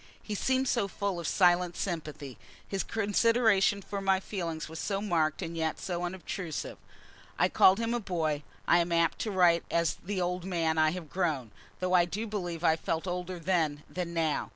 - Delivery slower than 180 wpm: No, average, 195 wpm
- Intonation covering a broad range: No, average, 3.0 semitones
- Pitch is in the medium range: Yes, medium, 175 Hz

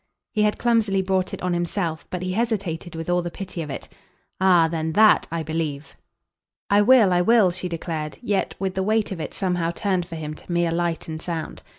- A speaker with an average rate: No, fast, 215 wpm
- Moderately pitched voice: Yes, medium, 180 Hz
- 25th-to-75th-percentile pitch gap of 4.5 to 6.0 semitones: No, average, 2.9 semitones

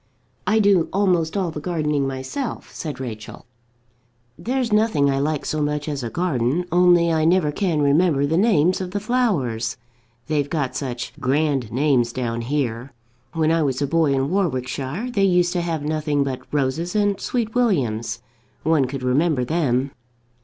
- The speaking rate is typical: Yes, average, 160 wpm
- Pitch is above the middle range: No, medium, 150 Hz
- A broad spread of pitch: No, average, 5.0 semitones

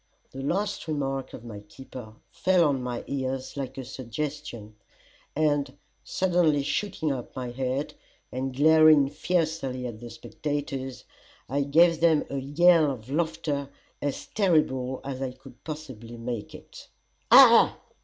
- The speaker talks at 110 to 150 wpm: Yes, slow, 135 wpm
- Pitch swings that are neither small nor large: Yes, average, 3.3 semitones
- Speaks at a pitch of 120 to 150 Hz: Yes, medium, 140 Hz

